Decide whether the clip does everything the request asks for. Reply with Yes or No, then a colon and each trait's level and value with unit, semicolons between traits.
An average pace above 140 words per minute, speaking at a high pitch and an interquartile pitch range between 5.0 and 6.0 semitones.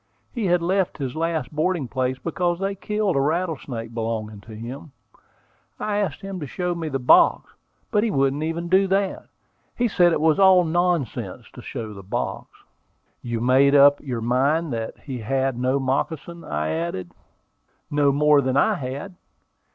No: average, 170 wpm; medium, 145 Hz; wide, 5.6 semitones